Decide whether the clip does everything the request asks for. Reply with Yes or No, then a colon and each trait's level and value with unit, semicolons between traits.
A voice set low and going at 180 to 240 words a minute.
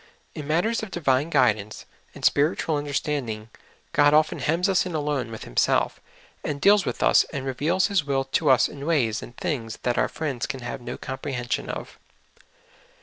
No: medium, 145 Hz; average, 195 wpm